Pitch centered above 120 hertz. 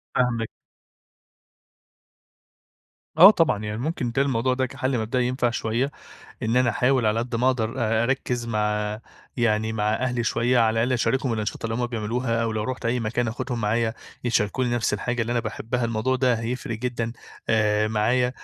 No: low, 115 Hz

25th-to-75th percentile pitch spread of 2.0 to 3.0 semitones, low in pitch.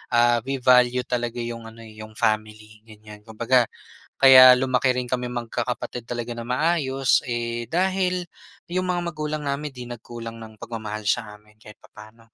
Yes: narrow, 2.6 semitones; low, 120 Hz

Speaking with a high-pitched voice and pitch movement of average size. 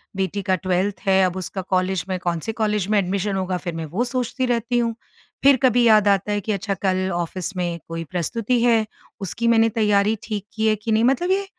Yes: high, 205 Hz; average, 3.5 semitones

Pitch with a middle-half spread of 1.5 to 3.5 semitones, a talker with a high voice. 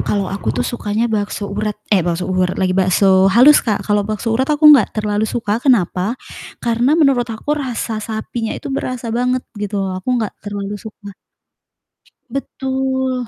No: average, 4.0 semitones; high, 220 Hz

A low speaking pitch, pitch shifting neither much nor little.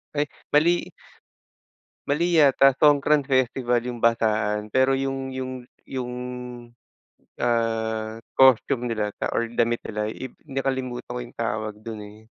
Yes: low, 125 Hz; average, 3.0 semitones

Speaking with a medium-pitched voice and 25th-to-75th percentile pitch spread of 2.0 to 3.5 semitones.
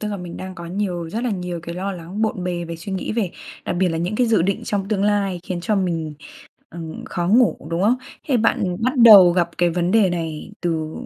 Yes: medium, 180 Hz; average, 3.2 semitones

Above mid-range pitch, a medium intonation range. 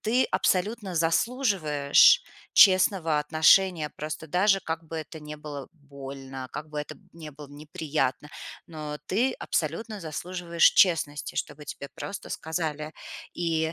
No: medium, 160 Hz; average, 3.5 semitones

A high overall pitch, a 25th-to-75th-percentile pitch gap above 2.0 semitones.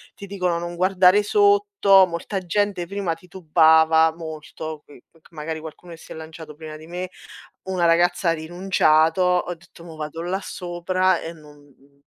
No: medium, 170 Hz; narrow, 2.6 semitones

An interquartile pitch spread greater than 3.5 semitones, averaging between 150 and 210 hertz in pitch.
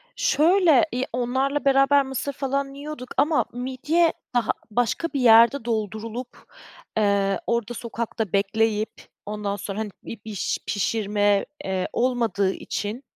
No: average, 4.5 semitones; high, 235 Hz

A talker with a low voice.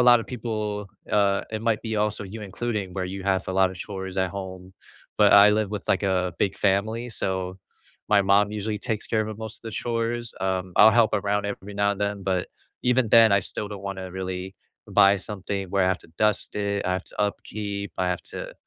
Yes: low, 100 Hz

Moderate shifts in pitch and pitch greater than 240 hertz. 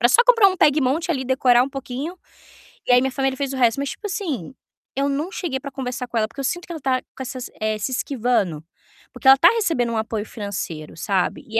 Yes: average, 3.6 semitones; very high, 260 Hz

